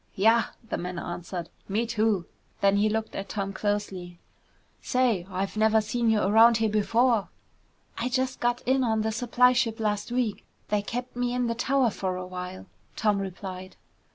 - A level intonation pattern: No, average, 3.4 semitones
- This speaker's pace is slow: No, average, 175 wpm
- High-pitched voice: Yes, high, 215 Hz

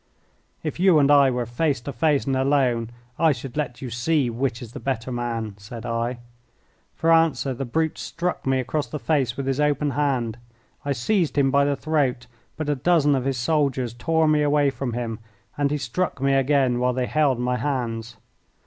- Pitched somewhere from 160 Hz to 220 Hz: No, low, 135 Hz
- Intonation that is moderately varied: Yes, average, 3.3 semitones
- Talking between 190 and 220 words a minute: Yes, average, 200 wpm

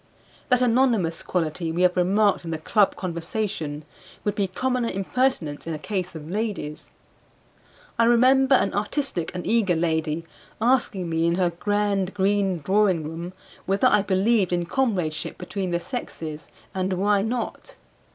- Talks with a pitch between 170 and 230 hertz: Yes, high, 190 Hz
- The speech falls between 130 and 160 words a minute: Yes, average, 150 wpm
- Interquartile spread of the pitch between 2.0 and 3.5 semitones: No, average, 4.4 semitones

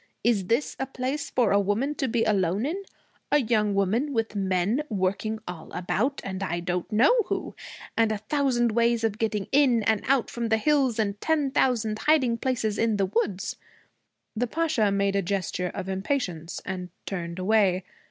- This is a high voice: Yes, high, 220 Hz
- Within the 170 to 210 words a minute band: Yes, average, 180 wpm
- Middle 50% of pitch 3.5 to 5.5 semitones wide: Yes, average, 4.5 semitones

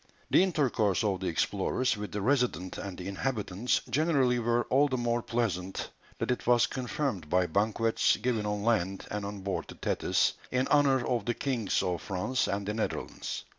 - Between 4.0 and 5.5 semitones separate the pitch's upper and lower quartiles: Yes, average, 4.3 semitones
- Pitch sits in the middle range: No, low, 115 Hz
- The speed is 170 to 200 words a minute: Yes, average, 180 wpm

